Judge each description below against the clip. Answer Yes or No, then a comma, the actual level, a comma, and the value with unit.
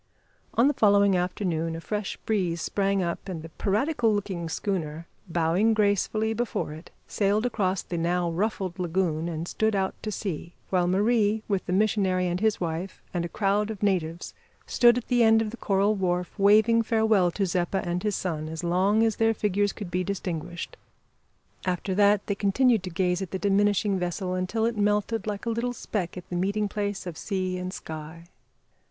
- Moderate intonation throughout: Yes, average, 3.1 semitones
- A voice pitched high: Yes, high, 195 Hz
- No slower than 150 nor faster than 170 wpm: No, average, 190 wpm